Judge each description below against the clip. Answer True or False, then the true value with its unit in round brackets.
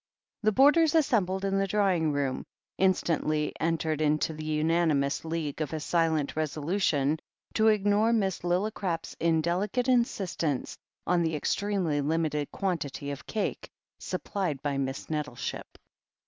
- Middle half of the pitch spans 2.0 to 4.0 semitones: False (4.5 semitones)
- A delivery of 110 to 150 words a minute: True (135 wpm)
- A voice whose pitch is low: False (165 Hz)